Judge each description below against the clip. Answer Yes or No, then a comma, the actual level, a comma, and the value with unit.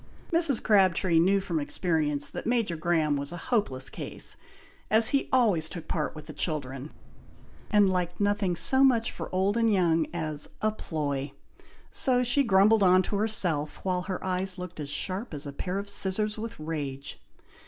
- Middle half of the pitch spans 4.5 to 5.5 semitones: Yes, average, 5.2 semitones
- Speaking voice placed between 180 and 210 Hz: Yes, medium, 185 Hz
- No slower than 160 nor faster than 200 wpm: Yes, average, 175 wpm